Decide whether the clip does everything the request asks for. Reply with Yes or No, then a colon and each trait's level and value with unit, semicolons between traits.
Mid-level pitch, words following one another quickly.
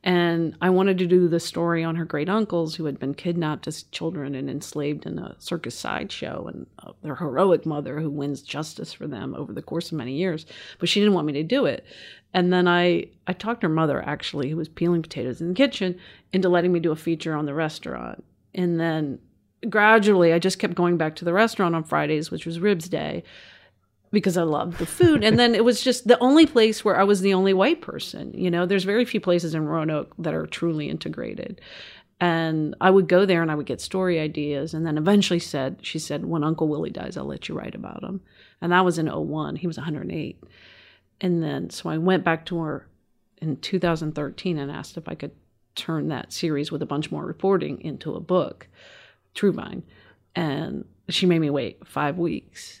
Yes: medium, 170 Hz; fast, 215 wpm